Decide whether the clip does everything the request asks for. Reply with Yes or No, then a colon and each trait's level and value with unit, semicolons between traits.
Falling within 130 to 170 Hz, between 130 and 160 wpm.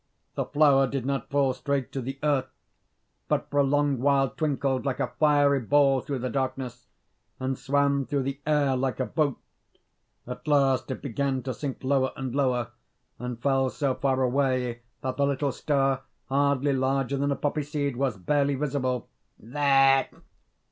No: low, 135 Hz; average, 170 wpm